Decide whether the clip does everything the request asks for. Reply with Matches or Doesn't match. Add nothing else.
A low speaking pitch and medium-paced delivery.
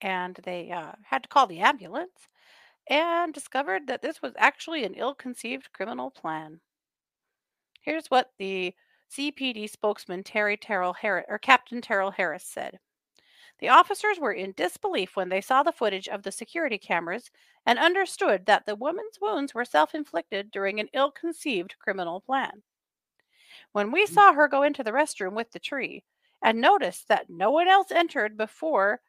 Doesn't match